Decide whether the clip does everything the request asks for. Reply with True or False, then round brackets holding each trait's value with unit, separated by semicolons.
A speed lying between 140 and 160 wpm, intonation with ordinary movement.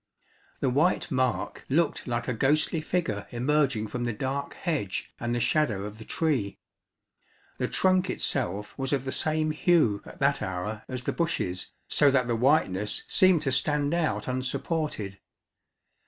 False (155 wpm; 5.7 semitones)